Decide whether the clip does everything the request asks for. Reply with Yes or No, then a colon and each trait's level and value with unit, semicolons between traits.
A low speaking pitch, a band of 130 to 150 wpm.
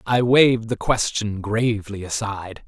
Yes: low, 110 Hz; slow, 135 wpm